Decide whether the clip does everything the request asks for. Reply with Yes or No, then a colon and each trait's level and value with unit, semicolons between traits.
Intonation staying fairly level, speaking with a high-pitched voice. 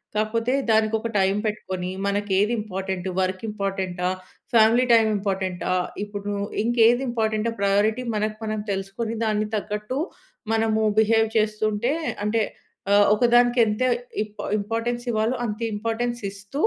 Yes: narrow, 2.2 semitones; high, 215 Hz